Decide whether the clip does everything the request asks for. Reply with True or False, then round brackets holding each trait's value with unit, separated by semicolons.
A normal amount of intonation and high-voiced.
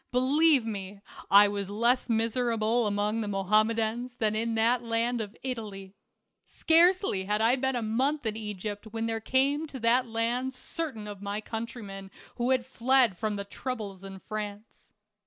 True (3.2 semitones; 225 Hz)